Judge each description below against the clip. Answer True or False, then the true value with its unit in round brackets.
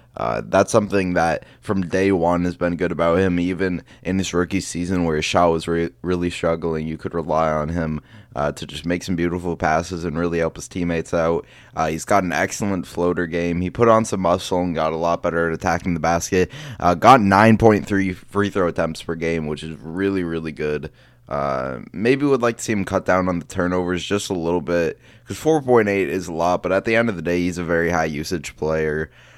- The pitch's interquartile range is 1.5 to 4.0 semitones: True (2.5 semitones)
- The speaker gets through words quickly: True (225 wpm)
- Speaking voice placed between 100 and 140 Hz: False (90 Hz)